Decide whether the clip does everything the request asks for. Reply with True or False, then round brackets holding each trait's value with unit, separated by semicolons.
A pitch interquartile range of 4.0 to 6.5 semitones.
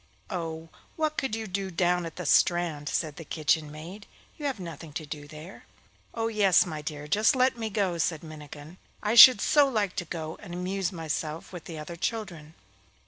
True (4.7 semitones)